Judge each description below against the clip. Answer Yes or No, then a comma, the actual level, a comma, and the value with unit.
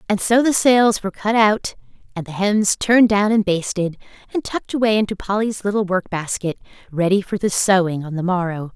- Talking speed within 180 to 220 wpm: Yes, average, 200 wpm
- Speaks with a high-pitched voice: Yes, high, 200 Hz